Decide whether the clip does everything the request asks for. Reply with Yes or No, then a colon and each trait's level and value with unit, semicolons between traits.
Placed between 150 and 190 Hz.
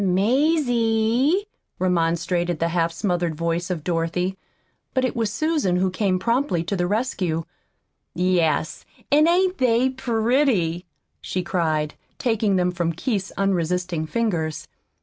Yes: medium, 185 Hz